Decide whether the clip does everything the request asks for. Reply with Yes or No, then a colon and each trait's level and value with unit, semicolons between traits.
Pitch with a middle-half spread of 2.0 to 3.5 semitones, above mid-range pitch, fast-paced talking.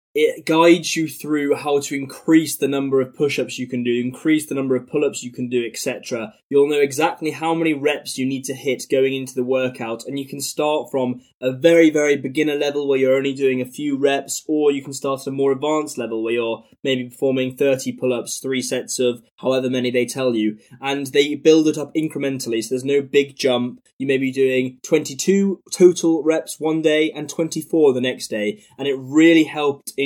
No: average, 2.8 semitones; medium, 140 Hz; fast, 220 wpm